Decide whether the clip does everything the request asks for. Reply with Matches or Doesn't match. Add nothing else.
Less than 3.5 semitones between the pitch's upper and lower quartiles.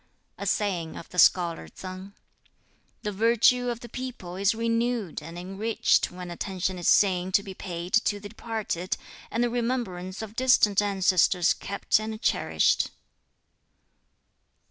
Doesn't match